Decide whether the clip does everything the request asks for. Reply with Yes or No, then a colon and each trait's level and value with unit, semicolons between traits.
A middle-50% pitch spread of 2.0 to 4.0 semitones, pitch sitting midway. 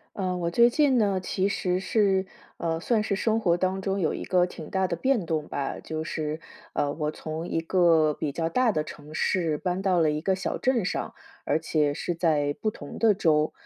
Yes: average, 3.7 semitones; medium, 175 Hz